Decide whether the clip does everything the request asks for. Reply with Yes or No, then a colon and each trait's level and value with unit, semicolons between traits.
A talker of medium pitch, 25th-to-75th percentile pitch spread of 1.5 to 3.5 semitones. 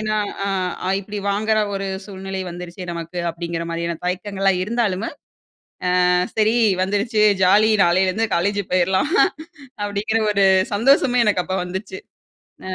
No: high, 195 Hz; average, 2.9 semitones